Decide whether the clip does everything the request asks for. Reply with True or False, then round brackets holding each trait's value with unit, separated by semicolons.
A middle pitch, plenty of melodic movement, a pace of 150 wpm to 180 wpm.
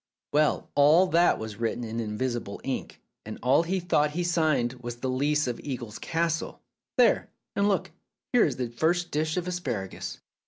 True (145 Hz; 6.0 semitones; 170 wpm)